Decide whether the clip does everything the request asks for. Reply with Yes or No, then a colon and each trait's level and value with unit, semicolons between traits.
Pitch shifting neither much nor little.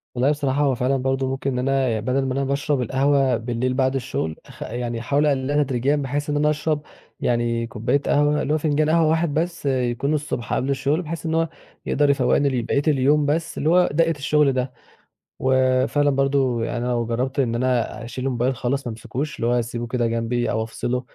Yes: average, 3.0 semitones